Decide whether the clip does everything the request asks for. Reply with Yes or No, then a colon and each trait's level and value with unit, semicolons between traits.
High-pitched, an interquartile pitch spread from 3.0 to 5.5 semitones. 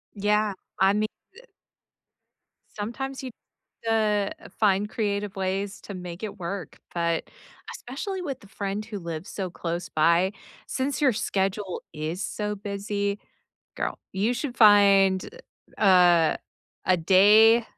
No: high, 200 Hz; narrow, 2.4 semitones